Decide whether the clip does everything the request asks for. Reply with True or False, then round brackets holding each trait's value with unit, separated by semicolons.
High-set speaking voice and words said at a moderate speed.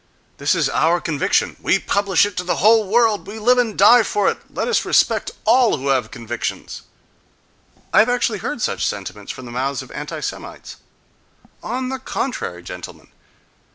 True (205 Hz; 165 wpm)